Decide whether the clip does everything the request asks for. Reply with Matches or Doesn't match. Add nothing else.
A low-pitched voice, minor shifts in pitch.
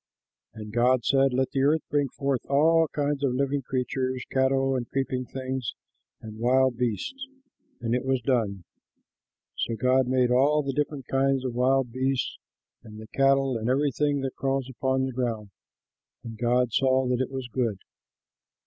Matches